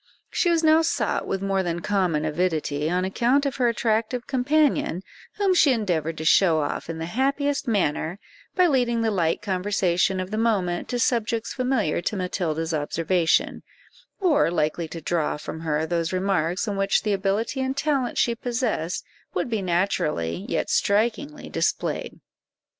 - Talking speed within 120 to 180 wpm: Yes, average, 160 wpm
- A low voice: No, high, 195 Hz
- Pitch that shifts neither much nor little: No, wide, 6.4 semitones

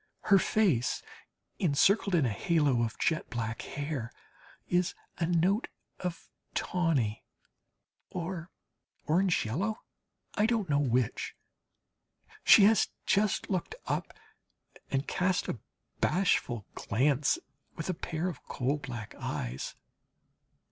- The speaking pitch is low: No, medium, 160 Hz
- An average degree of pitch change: No, wide, 6.5 semitones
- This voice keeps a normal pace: No, slow, 115 wpm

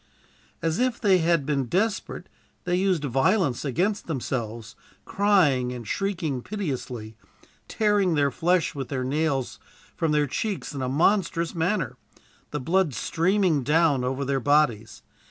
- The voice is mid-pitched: Yes, medium, 155 Hz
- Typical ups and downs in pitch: No, wide, 5.9 semitones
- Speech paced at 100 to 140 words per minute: Yes, slow, 135 wpm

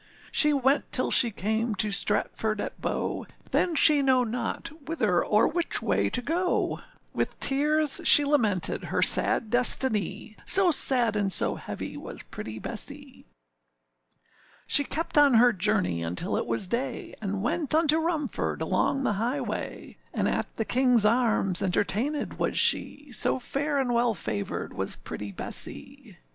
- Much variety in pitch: Yes, wide, 5.7 semitones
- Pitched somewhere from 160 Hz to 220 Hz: No, high, 245 Hz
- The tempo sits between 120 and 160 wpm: Yes, average, 150 wpm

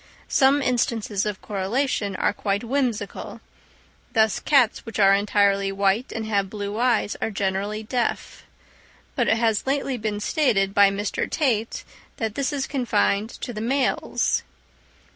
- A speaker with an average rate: Yes, average, 145 wpm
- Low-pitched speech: No, high, 215 Hz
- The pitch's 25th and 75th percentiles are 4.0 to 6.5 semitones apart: No, average, 3.6 semitones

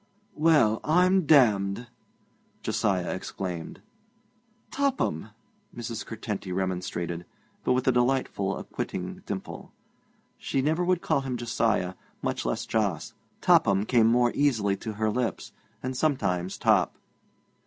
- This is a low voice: Yes, low, 115 Hz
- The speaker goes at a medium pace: No, slow, 115 wpm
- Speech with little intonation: No, wide, 5.5 semitones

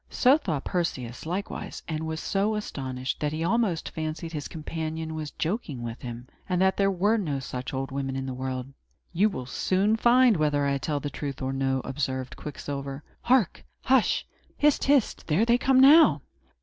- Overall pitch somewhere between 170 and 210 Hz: No, medium, 155 Hz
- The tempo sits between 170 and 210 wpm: Yes, average, 180 wpm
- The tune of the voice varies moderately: No, wide, 6.9 semitones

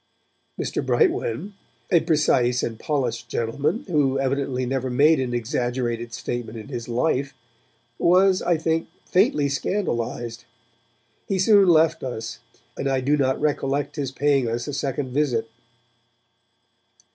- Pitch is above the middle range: No, low, 135 Hz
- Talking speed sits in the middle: No, slow, 130 wpm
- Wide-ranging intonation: No, average, 4.4 semitones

